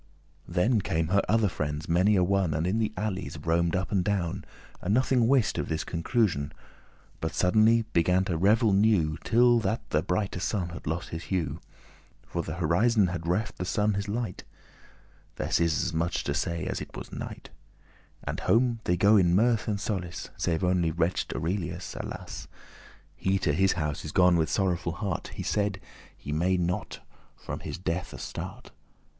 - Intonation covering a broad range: No, average, 3.6 semitones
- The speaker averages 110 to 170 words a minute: No, average, 180 wpm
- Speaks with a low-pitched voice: Yes, very low, 90 Hz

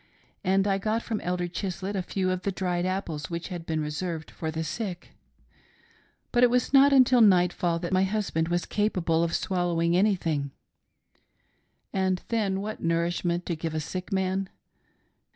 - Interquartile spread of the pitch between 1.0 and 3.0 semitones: Yes, narrow, 2.6 semitones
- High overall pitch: No, medium, 180 Hz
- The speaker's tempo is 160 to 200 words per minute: Yes, average, 170 wpm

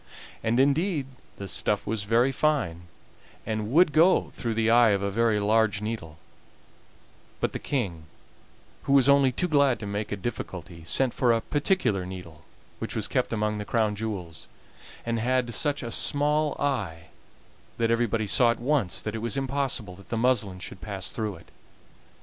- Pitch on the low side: Yes, low, 115 Hz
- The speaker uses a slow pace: No, average, 175 wpm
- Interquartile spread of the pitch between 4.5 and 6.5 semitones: Yes, average, 4.9 semitones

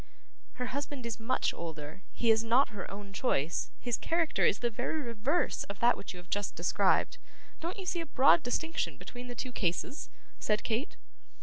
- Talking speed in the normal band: Yes, average, 190 wpm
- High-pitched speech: Yes, high, 235 Hz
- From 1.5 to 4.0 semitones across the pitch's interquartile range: No, average, 5.3 semitones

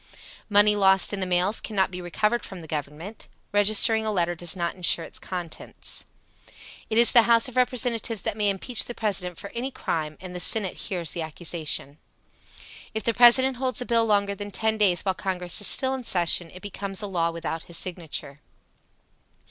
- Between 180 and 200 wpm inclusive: Yes, average, 190 wpm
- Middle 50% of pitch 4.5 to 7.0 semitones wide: No, average, 4.1 semitones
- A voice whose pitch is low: No, high, 195 Hz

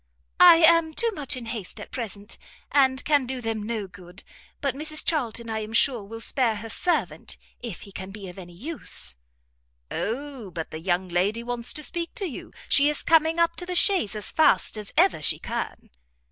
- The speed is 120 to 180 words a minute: No, average, 200 wpm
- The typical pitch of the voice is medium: No, high, 235 Hz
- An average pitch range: No, wide, 7.1 semitones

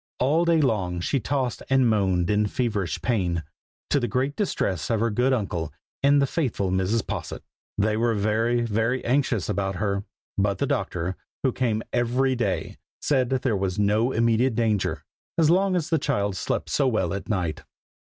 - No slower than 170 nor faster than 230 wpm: Yes, average, 180 wpm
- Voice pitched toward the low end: Yes, low, 115 Hz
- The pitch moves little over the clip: No, average, 4.8 semitones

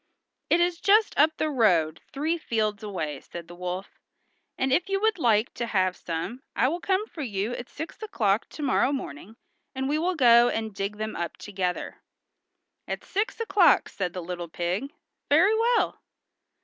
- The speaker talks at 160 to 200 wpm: Yes, average, 175 wpm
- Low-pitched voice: No, high, 235 Hz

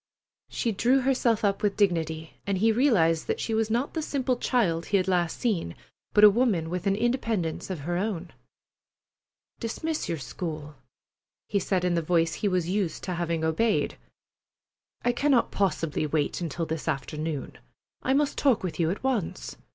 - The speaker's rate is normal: Yes, average, 175 wpm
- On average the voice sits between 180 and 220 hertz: Yes, high, 190 Hz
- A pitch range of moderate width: No, wide, 5.8 semitones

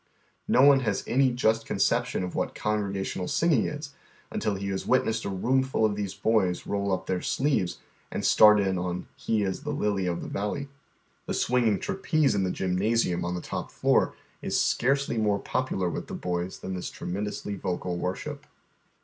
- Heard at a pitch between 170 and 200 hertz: No, low, 105 Hz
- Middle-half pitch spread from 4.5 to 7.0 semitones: Yes, average, 5.0 semitones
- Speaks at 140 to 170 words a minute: No, average, 185 wpm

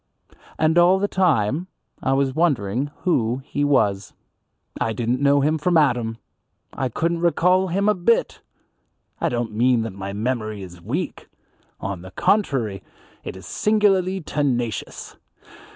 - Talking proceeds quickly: No, average, 140 wpm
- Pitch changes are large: Yes, wide, 7.5 semitones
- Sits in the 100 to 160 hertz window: Yes, low, 135 Hz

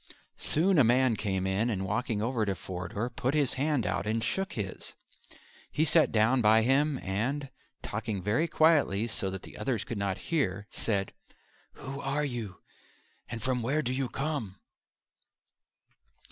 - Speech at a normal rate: Yes, average, 160 wpm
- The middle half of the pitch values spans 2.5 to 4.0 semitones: No, average, 5.2 semitones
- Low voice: Yes, low, 115 Hz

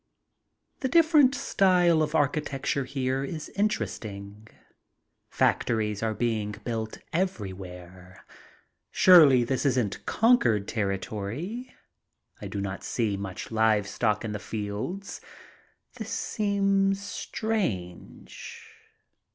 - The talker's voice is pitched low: Yes, low, 120 Hz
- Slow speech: Yes, slow, 95 wpm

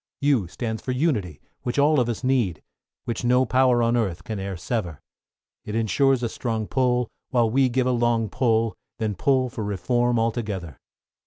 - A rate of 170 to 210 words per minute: Yes, average, 175 wpm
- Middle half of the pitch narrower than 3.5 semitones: Yes, average, 3.0 semitones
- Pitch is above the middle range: No, low, 120 Hz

